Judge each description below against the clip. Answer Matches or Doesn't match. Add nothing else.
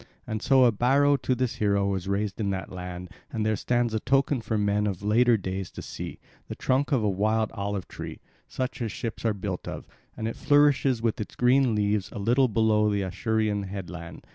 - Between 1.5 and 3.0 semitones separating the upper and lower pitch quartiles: Doesn't match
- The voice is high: Doesn't match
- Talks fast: Matches